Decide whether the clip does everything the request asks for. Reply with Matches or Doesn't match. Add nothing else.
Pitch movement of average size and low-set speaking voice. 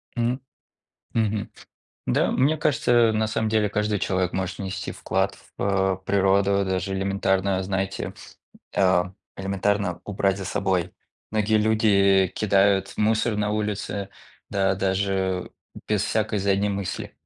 Doesn't match